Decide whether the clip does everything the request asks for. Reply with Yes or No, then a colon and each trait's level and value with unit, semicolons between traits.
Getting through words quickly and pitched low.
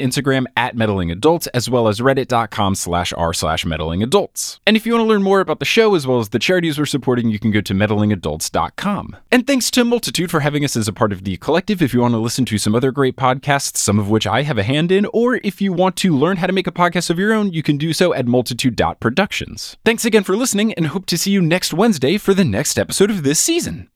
No: fast, 255 wpm; medium, 145 Hz